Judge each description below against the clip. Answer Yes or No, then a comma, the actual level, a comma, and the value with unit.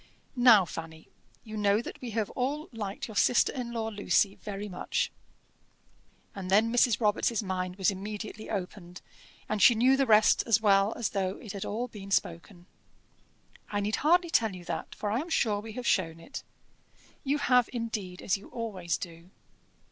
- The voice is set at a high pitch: Yes, high, 210 Hz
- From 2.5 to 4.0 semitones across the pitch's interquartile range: Yes, average, 3.2 semitones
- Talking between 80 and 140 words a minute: No, average, 180 wpm